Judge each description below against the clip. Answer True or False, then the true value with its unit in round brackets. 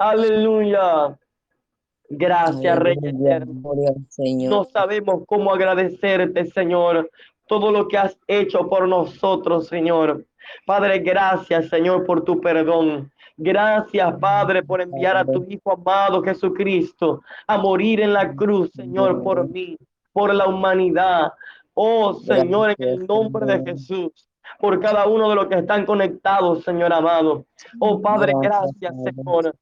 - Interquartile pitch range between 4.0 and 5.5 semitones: False (3.3 semitones)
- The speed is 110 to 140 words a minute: True (130 wpm)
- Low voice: False (185 Hz)